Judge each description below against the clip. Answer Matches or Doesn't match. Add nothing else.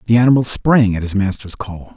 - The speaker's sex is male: Matches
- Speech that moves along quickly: Matches